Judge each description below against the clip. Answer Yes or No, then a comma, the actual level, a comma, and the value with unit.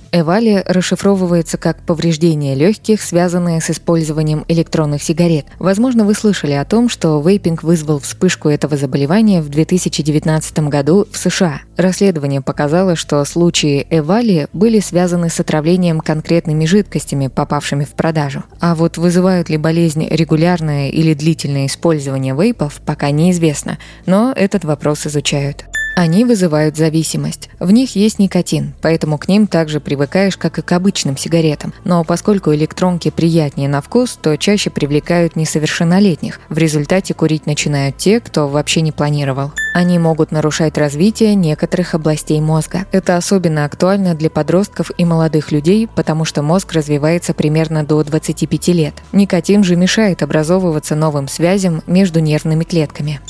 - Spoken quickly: No, average, 140 wpm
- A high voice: No, medium, 165 Hz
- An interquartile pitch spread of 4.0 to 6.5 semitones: No, average, 3.1 semitones